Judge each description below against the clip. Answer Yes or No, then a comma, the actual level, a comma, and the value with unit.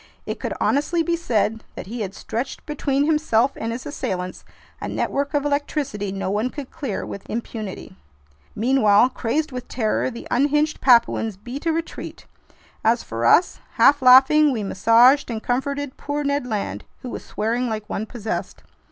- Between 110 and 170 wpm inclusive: Yes, average, 165 wpm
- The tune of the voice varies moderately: Yes, average, 4.7 semitones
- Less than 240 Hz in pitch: No, very high, 250 Hz